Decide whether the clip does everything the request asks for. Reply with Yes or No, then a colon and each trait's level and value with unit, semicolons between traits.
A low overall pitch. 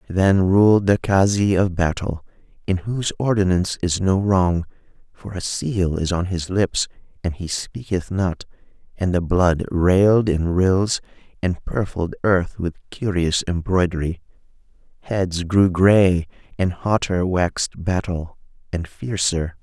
Yes: very low, 90 Hz